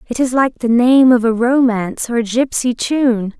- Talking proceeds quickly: Yes, fast, 210 wpm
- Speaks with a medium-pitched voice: No, high, 240 Hz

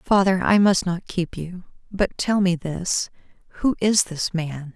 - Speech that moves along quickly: No, average, 165 wpm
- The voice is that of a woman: Yes, female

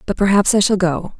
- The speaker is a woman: Yes, female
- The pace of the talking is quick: Yes, fast, 250 wpm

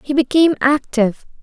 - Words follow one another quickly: No, slow, 125 wpm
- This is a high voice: Yes, very high, 275 Hz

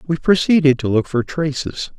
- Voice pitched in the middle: Yes, medium, 150 Hz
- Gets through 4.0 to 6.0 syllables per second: Yes, 5.0 syllables/s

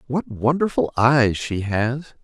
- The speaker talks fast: No, slow, 135 wpm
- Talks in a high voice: No, low, 125 Hz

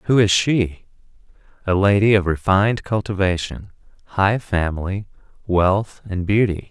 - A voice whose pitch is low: Yes, very low, 95 Hz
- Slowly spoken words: Yes, slow, 115 wpm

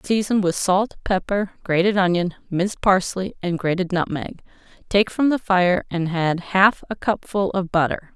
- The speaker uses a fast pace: No, average, 160 wpm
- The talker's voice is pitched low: No, medium, 185 Hz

